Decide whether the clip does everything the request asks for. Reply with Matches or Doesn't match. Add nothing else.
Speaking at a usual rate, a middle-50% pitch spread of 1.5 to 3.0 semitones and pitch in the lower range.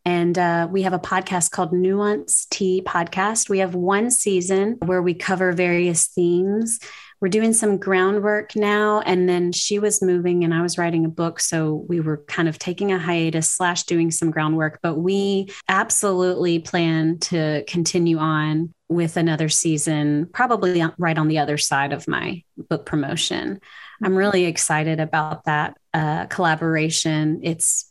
Doesn't match